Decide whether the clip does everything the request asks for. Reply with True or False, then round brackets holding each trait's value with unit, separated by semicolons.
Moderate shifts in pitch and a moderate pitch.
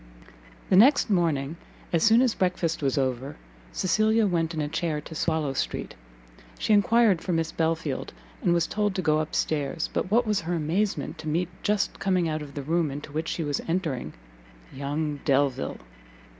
True (4.0 semitones; 165 Hz)